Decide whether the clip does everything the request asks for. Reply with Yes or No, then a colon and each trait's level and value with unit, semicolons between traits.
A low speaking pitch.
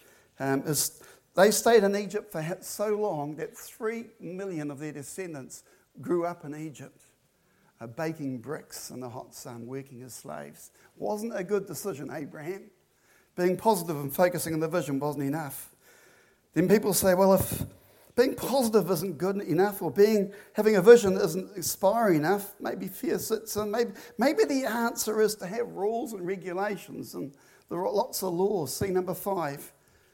No: medium, 185 Hz